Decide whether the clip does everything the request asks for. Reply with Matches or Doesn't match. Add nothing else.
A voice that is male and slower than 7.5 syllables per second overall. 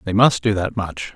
Matches